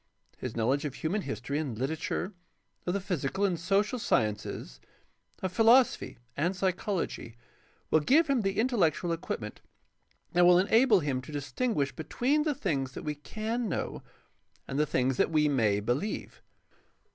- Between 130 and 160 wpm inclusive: Yes, average, 150 wpm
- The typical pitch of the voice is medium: Yes, medium, 170 Hz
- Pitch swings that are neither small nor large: No, wide, 7.4 semitones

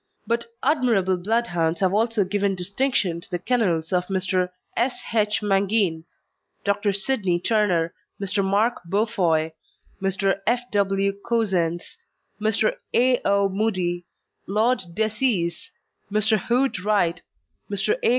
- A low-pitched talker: No, high, 200 Hz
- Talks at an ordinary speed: No, slow, 120 wpm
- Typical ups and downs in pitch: Yes, average, 3.5 semitones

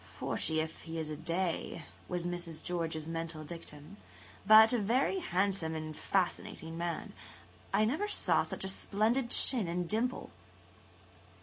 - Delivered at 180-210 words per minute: No, average, 140 wpm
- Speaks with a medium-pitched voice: Yes, medium, 175 Hz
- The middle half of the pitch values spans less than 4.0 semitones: No, average, 4.8 semitones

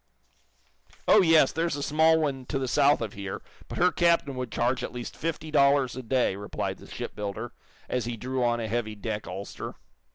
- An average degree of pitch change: Yes, average, 4.5 semitones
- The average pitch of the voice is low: Yes, low, 130 Hz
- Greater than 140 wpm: Yes, average, 195 wpm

